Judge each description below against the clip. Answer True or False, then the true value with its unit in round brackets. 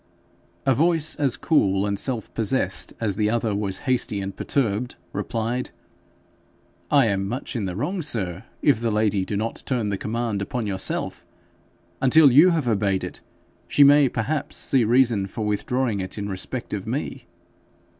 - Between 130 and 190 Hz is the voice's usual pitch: False (115 Hz)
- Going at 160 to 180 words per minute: True (165 wpm)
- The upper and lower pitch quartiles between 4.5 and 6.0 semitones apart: True (4.8 semitones)